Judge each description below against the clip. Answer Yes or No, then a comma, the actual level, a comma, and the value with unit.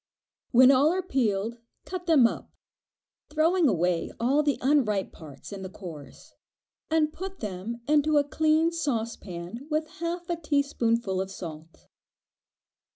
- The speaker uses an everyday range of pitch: No, wide, 8.0 semitones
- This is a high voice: Yes, very high, 260 Hz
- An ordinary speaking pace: No, slow, 130 wpm